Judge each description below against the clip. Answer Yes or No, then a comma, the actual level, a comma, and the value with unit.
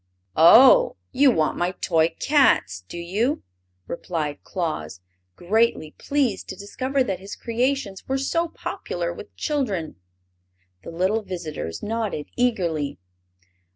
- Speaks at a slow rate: Yes, slow, 120 wpm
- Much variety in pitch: Yes, wide, 7.6 semitones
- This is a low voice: No, high, 195 Hz